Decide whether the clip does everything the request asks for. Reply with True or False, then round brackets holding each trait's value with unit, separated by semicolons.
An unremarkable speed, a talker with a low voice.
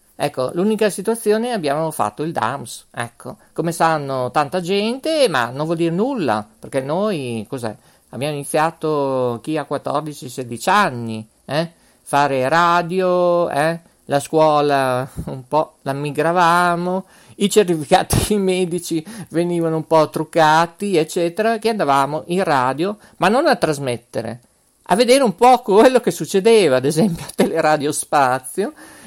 False (135 wpm; 160 Hz)